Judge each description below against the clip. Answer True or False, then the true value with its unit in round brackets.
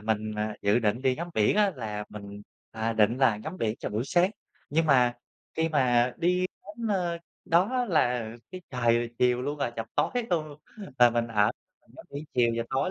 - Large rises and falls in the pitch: True (6.6 semitones)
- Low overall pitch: True (125 Hz)